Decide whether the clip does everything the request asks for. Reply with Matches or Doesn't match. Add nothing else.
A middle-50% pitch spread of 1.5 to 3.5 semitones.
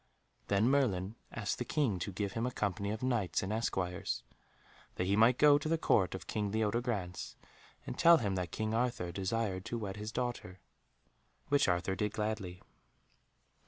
Doesn't match